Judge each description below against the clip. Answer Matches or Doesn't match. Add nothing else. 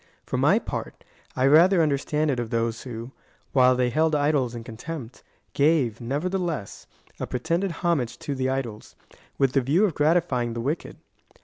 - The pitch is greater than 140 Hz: Doesn't match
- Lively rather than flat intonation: Doesn't match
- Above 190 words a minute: Doesn't match